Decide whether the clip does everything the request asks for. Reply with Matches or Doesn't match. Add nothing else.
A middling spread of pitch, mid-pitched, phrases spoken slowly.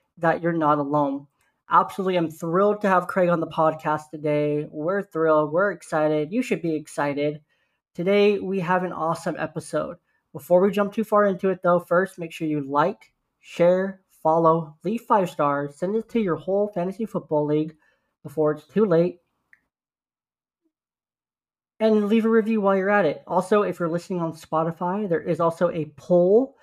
Doesn't match